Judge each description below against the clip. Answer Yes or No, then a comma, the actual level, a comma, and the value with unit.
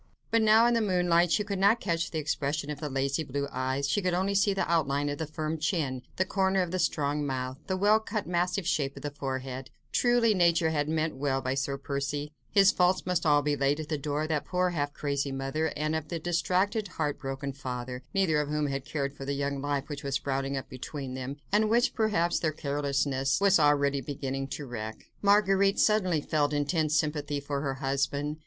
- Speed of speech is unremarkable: No, fast, 220 wpm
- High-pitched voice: No, medium, 150 Hz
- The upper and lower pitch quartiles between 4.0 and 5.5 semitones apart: Yes, average, 4.4 semitones